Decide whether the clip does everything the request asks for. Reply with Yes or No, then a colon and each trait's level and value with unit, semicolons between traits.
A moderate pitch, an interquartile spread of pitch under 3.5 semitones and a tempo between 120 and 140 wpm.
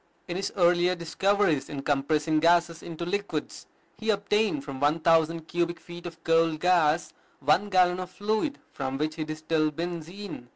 No: medium, 170 Hz; average, 2.8 semitones; average, 160 wpm